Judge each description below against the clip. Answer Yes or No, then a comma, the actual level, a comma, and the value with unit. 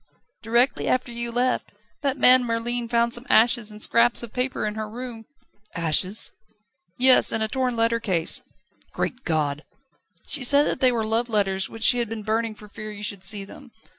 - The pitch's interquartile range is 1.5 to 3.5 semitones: Yes, narrow, 2.5 semitones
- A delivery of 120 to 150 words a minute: No, average, 195 wpm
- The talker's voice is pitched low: No, high, 230 Hz